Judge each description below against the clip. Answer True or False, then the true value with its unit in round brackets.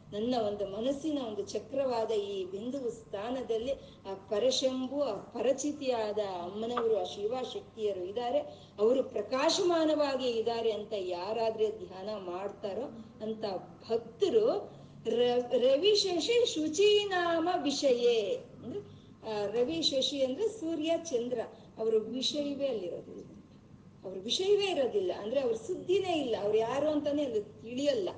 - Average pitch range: False (7.0 semitones)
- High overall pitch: True (250 Hz)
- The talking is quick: True (110 wpm)